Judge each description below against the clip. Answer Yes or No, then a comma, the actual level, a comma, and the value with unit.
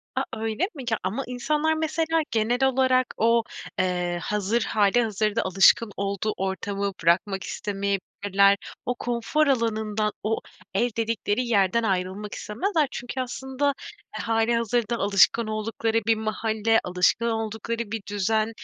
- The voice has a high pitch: Yes, high, 220 Hz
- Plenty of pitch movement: No, average, 3.1 semitones